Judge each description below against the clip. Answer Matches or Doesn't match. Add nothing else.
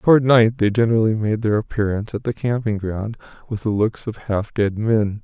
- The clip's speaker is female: Doesn't match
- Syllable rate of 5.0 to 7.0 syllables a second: Matches